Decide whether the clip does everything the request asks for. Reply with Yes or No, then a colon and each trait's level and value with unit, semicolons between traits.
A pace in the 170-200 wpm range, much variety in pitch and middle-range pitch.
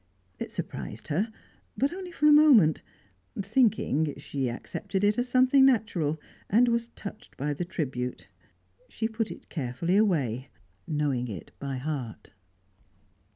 No: slow, 135 wpm; wide, 8.9 semitones; medium, 175 Hz